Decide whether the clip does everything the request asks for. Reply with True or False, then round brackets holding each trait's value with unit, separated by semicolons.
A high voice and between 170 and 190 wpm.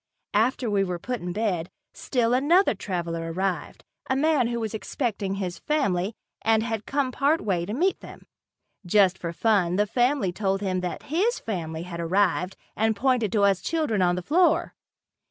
True (205 Hz; 175 wpm)